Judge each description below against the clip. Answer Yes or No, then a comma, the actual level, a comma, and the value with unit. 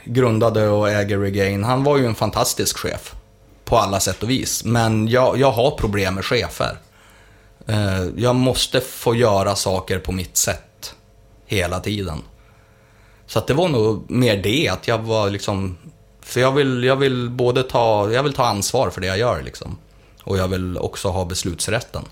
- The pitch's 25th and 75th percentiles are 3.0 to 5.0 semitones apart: Yes, average, 3.3 semitones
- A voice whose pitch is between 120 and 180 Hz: No, low, 110 Hz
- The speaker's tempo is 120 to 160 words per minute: No, average, 180 wpm